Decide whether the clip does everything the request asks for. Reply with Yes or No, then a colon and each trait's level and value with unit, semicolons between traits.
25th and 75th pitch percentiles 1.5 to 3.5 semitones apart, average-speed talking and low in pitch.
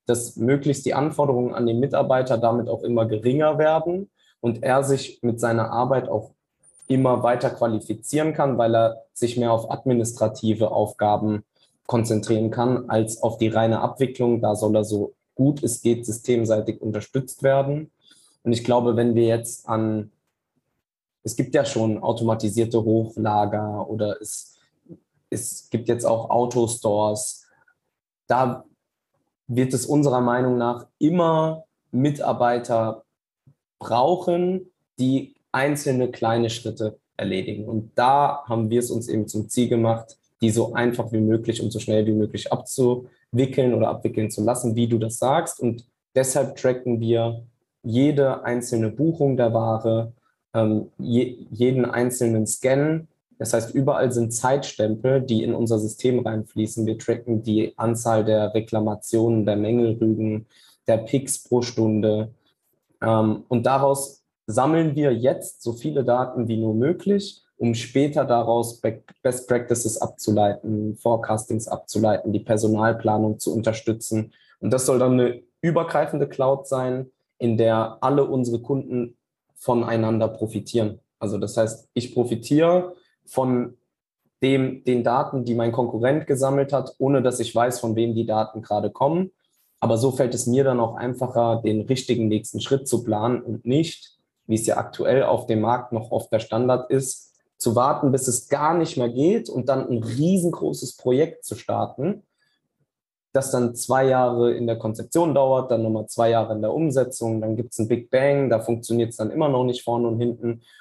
Yes: average, 2.9 semitones; average, 150 wpm; low, 120 Hz